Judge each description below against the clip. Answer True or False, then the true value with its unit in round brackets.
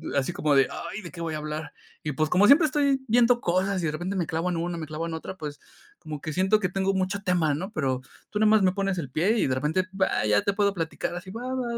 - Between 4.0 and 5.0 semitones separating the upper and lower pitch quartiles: True (4.4 semitones)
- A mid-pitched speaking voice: True (180 Hz)